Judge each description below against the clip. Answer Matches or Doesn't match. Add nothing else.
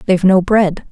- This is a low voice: Doesn't match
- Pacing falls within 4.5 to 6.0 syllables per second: Matches